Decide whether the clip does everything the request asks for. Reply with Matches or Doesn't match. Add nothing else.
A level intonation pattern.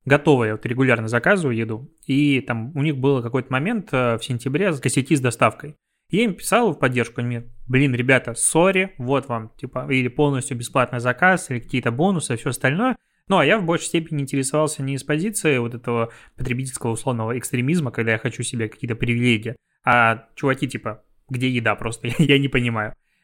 Doesn't match